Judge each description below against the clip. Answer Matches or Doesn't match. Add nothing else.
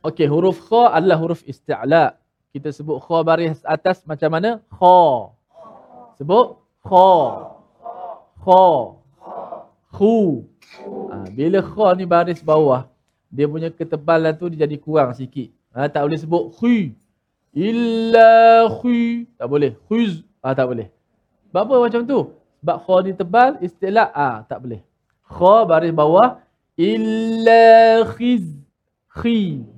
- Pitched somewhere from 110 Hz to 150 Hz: Doesn't match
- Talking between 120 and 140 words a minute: Matches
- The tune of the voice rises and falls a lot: Matches